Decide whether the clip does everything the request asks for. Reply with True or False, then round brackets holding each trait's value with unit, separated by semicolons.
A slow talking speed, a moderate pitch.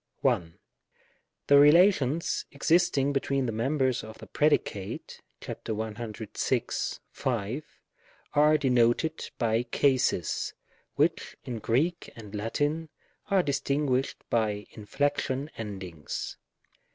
False (90 wpm; 130 Hz)